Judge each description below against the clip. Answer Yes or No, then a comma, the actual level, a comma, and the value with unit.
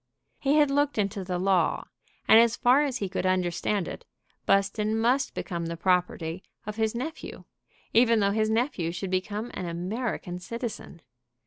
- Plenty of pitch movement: No, average, 4.4 semitones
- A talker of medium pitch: No, high, 210 Hz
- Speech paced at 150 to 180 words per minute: Yes, average, 160 wpm